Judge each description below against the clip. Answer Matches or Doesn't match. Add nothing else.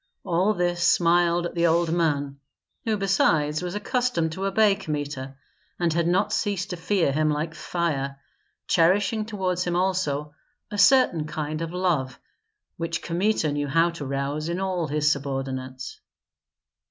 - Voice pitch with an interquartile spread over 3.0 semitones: Matches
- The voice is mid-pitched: Matches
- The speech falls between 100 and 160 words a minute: Matches